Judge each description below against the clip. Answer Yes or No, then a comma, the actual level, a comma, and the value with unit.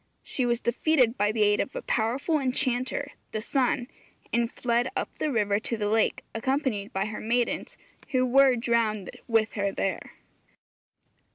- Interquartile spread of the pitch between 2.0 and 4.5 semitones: Yes, average, 3.1 semitones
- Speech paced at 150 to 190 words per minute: Yes, average, 160 wpm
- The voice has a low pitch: No, high, 235 Hz